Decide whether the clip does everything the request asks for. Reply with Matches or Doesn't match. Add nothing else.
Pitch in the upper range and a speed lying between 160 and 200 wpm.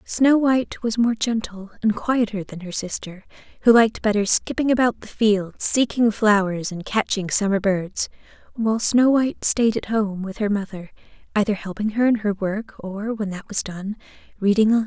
Matches